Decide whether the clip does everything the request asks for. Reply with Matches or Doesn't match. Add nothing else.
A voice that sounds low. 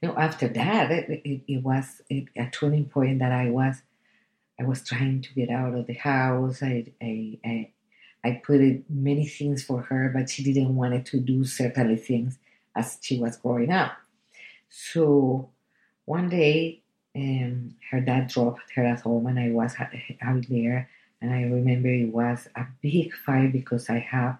Matches